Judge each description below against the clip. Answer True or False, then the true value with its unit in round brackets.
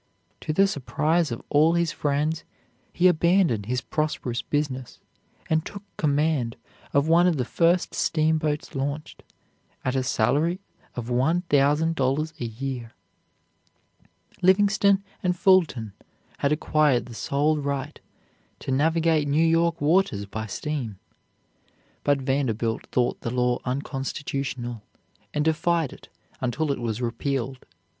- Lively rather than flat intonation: False (4.3 semitones)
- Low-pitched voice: False (145 Hz)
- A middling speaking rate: False (125 wpm)